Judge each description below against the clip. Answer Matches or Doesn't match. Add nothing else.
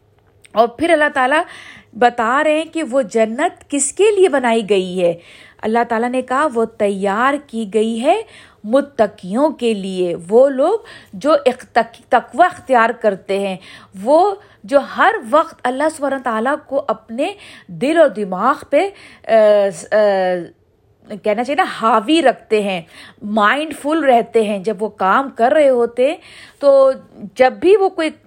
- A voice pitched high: Matches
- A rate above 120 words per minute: Matches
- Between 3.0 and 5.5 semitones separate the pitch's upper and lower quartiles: Doesn't match